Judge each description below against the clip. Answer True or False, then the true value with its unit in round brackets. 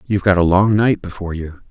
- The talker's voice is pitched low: True (95 Hz)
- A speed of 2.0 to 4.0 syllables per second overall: False (6.5 syllables/s)